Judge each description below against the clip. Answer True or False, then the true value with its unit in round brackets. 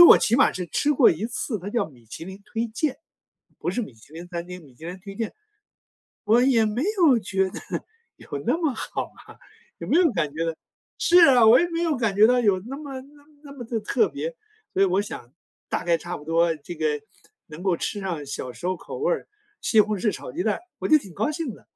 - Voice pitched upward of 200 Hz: True (210 Hz)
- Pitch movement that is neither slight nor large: False (7.5 semitones)